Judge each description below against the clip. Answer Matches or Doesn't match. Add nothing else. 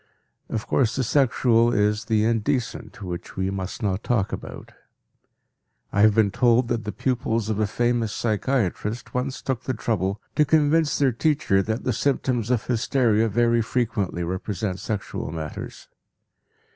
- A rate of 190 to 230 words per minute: Doesn't match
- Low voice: Matches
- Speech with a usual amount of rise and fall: Matches